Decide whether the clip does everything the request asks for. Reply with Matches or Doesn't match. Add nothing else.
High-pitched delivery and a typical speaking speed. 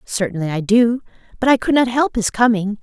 Matches